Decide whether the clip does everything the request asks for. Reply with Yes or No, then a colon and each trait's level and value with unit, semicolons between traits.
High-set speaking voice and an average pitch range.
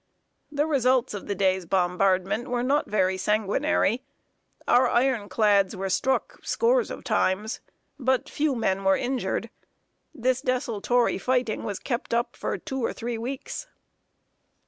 Yes: high, 235 Hz; average, 4.8 semitones